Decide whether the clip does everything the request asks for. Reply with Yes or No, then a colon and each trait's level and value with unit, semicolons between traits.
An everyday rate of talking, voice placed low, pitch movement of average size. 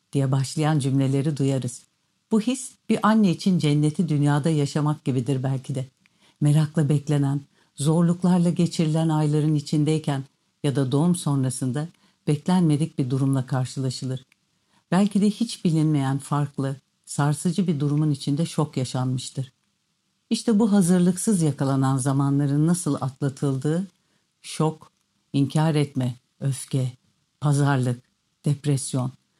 No: average, 110 wpm; medium, 150 Hz; average, 3.9 semitones